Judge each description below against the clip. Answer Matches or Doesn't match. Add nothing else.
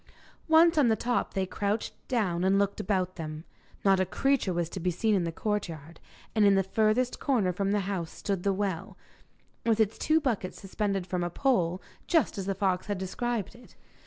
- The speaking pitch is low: Doesn't match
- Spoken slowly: Doesn't match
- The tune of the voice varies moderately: Matches